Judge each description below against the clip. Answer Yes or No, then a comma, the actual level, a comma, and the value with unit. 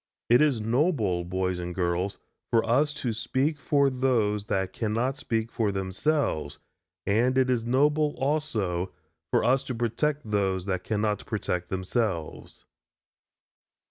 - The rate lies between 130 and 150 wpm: Yes, slow, 135 wpm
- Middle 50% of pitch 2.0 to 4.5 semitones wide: No, wide, 5.5 semitones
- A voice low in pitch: Yes, low, 115 Hz